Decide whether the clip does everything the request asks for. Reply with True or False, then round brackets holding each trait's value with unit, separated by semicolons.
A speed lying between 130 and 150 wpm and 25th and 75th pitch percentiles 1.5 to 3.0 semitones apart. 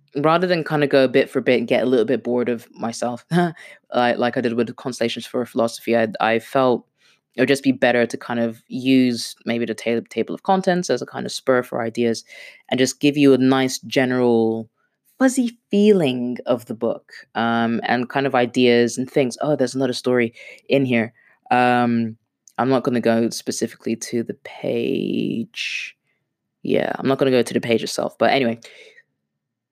False (195 wpm; 2.7 semitones)